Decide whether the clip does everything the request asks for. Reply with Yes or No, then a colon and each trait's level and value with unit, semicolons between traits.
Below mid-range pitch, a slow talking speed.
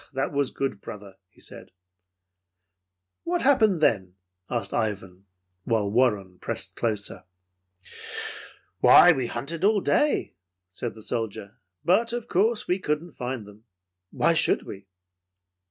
Yes: low, 120 Hz; slow, 125 wpm